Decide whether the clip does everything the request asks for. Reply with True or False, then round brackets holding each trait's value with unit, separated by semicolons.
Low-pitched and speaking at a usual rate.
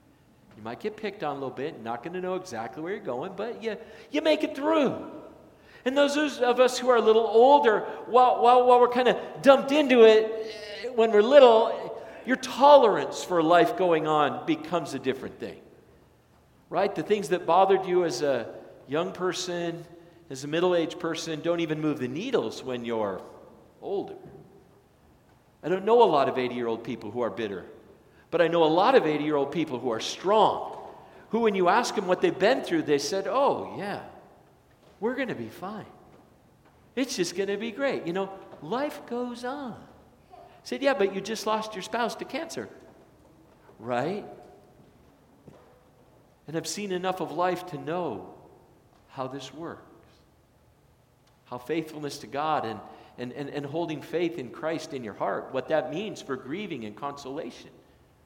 False (180 Hz; 175 wpm)